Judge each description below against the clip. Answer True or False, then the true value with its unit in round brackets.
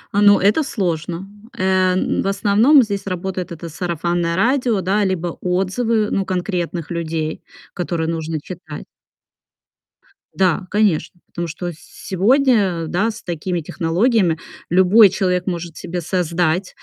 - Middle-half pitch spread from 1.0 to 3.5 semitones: True (2.9 semitones)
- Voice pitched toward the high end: False (180 Hz)